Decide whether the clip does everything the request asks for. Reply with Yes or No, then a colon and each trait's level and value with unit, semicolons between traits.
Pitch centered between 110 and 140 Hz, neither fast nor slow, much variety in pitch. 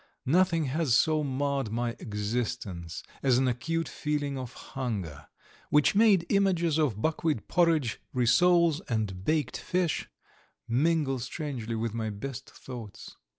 No: low, 135 Hz; slow, 125 wpm; wide, 5.7 semitones